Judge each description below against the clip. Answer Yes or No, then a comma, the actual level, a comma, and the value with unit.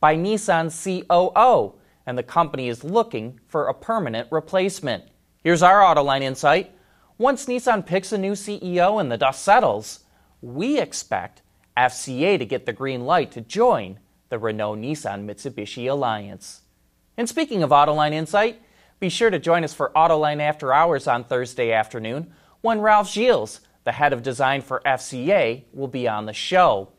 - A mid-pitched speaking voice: Yes, medium, 150 Hz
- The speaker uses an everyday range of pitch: No, wide, 7.5 semitones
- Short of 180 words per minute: Yes, average, 160 wpm